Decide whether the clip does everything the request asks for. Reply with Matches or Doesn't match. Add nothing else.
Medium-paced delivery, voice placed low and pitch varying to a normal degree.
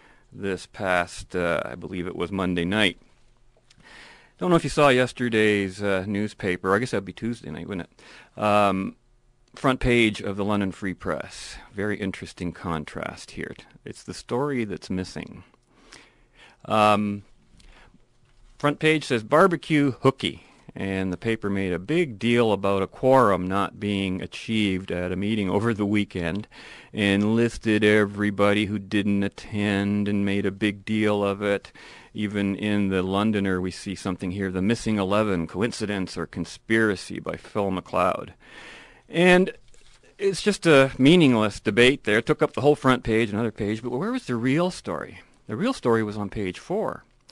Matches